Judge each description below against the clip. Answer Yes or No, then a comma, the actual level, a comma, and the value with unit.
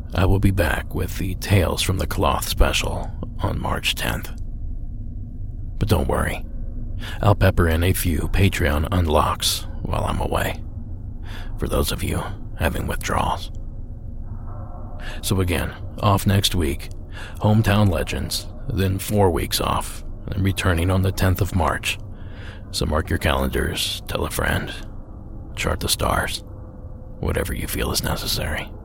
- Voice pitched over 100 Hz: No, very low, 95 Hz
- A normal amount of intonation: Yes, average, 3.0 semitones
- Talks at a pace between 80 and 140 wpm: Yes, slow, 135 wpm